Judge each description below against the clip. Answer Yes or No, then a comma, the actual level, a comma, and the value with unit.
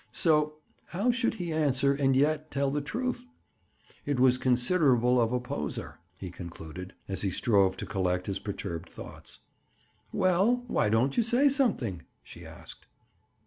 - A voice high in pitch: No, low, 135 Hz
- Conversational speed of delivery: Yes, average, 150 wpm